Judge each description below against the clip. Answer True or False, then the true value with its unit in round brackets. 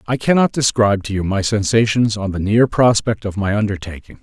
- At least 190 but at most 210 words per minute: True (200 wpm)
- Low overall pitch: True (105 Hz)